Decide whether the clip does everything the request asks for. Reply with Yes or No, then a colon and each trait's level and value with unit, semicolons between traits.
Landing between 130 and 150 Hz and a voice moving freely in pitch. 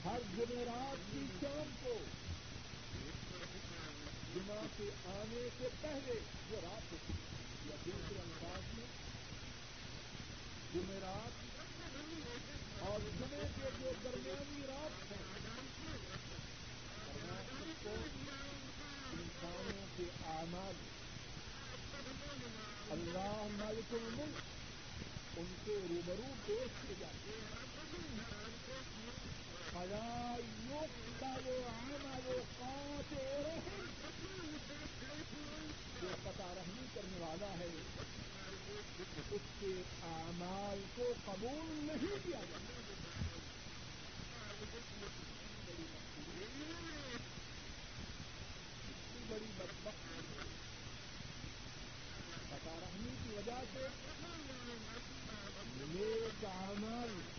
No: high, 210 Hz; wide, 7.2 semitones